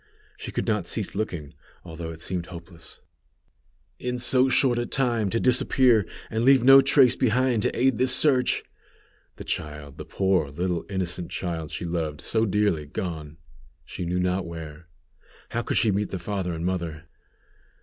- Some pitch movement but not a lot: No, wide, 6.3 semitones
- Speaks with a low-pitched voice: Yes, very low, 95 Hz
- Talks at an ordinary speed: Yes, average, 165 wpm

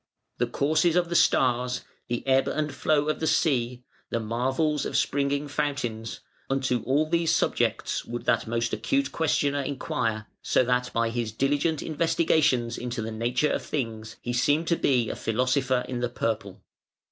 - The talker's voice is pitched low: Yes, low, 130 Hz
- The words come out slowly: No, average, 165 wpm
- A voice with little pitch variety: No, average, 3.9 semitones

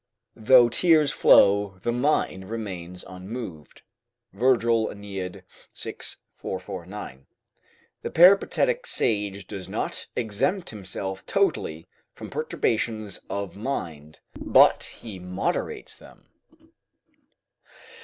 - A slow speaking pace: Yes, slow, 90 wpm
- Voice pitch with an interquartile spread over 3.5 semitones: Yes, average, 4.3 semitones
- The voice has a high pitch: No, low, 100 Hz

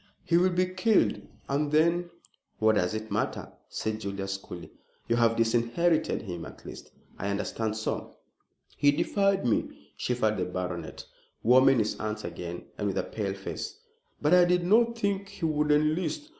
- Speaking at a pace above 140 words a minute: Yes, average, 170 wpm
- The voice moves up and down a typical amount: No, wide, 8.6 semitones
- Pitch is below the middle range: Yes, low, 125 Hz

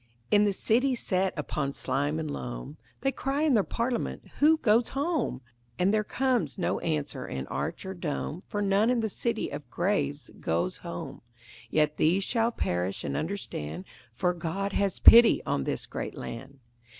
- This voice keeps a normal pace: Yes, average, 170 wpm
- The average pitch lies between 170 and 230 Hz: Yes, medium, 185 Hz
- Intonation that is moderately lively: No, wide, 7.8 semitones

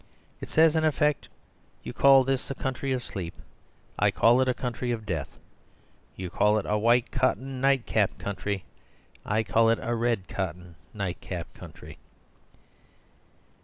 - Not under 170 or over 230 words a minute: No, average, 150 wpm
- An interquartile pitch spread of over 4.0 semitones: Yes, average, 4.6 semitones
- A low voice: Yes, low, 115 Hz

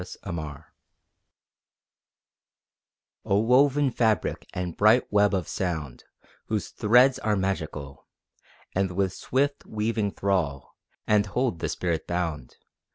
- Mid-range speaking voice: No, low, 100 Hz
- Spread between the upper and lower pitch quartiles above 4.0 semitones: Yes, average, 4.6 semitones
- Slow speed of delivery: Yes, slow, 115 wpm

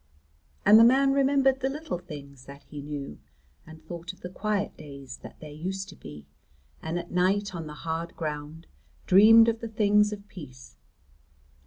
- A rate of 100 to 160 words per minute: No, average, 175 wpm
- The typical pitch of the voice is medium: Yes, medium, 180 Hz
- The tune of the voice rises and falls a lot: Yes, wide, 6.0 semitones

